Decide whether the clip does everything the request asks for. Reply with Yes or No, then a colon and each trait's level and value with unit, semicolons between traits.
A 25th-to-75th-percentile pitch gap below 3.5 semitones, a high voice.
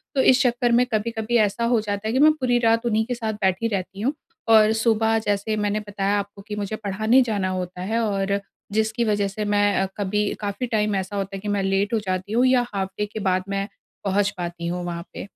Yes: narrow, 2.4 semitones; high, 210 Hz